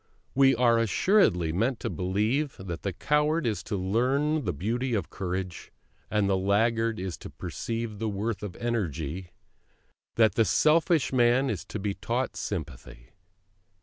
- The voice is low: Yes, low, 110 Hz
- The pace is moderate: Yes, average, 150 wpm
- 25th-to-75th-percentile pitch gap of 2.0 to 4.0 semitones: No, average, 4.8 semitones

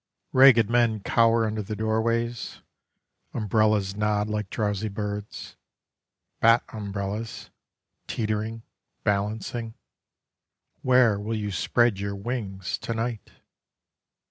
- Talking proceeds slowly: Yes, slow, 95 wpm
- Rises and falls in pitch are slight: Yes, narrow, 2.0 semitones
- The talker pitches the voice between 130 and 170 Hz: No, low, 110 Hz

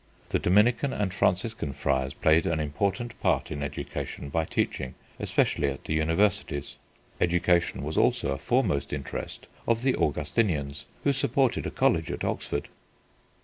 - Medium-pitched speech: No, very low, 80 Hz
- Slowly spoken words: No, average, 145 wpm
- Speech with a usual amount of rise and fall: No, wide, 6.5 semitones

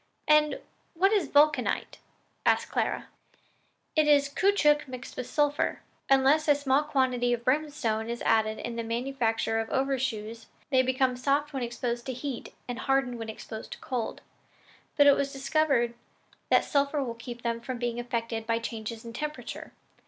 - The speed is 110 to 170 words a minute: Yes, average, 165 wpm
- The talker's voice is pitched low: No, very high, 255 Hz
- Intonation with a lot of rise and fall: No, average, 3.6 semitones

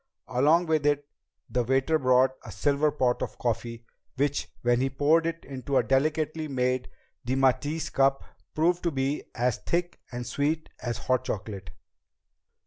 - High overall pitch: No, low, 135 Hz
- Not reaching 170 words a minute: Yes, average, 150 wpm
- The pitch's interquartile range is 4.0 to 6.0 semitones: No, average, 3.6 semitones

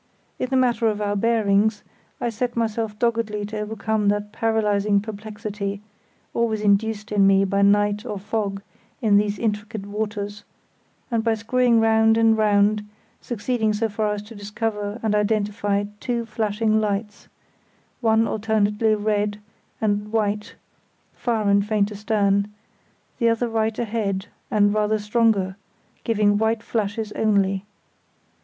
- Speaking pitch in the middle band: No, high, 210 Hz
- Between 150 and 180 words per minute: No, slow, 135 wpm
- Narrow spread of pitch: Yes, narrow, 1.5 semitones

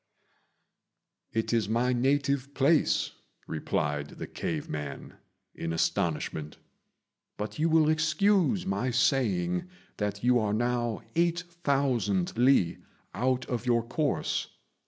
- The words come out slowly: Yes, slow, 110 wpm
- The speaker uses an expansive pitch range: Yes, wide, 6.0 semitones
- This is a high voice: No, low, 125 Hz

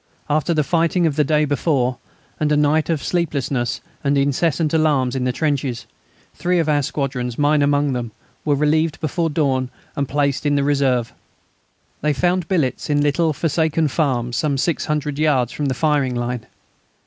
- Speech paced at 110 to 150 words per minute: No, average, 165 wpm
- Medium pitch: Yes, medium, 145 Hz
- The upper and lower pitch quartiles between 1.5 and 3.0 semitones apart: Yes, average, 2.7 semitones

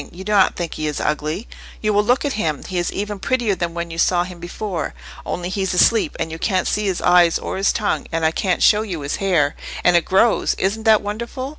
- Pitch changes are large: No, average, 3.6 semitones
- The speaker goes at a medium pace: No, fast, 230 wpm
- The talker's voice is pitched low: No, medium, 185 Hz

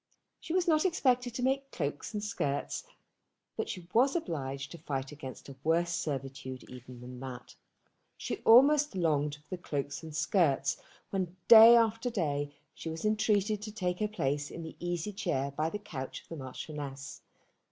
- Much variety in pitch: Yes, wide, 7.3 semitones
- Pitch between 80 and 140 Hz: No, medium, 165 Hz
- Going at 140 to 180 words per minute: Yes, average, 175 wpm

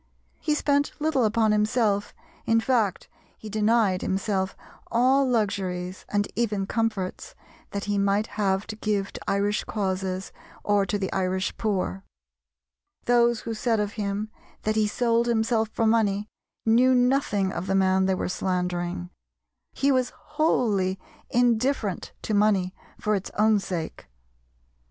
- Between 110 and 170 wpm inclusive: Yes, average, 140 wpm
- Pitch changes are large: No, average, 3.1 semitones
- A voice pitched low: No, high, 210 Hz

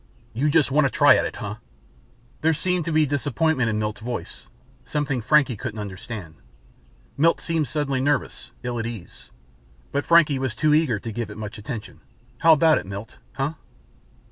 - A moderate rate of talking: Yes, average, 175 wpm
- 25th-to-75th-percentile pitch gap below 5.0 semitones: No, wide, 5.5 semitones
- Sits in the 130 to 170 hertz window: Yes, low, 135 Hz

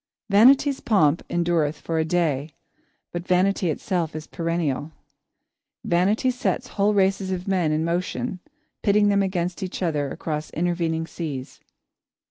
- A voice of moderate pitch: Yes, medium, 175 Hz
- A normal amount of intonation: Yes, average, 3.5 semitones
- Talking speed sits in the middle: No, slow, 130 wpm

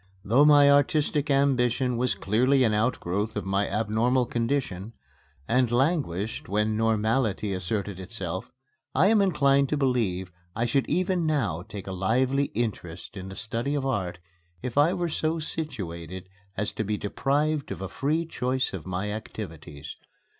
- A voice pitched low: Yes, low, 115 Hz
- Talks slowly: No, average, 155 wpm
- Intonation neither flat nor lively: No, wide, 5.8 semitones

